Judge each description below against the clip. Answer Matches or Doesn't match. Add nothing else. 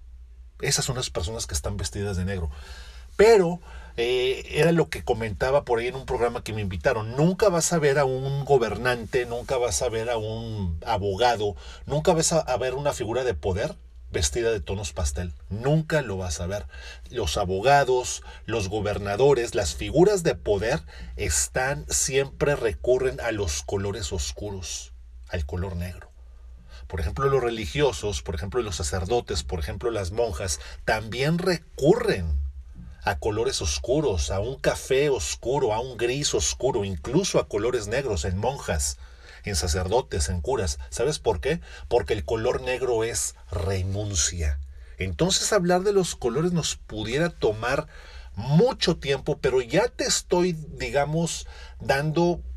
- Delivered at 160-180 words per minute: Doesn't match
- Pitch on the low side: Matches